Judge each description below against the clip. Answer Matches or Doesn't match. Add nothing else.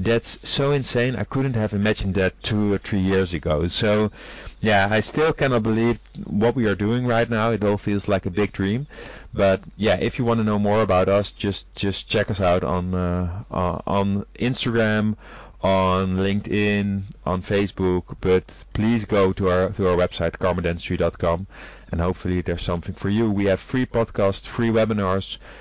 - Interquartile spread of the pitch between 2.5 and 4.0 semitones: Matches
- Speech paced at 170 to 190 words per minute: Matches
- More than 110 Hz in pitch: Doesn't match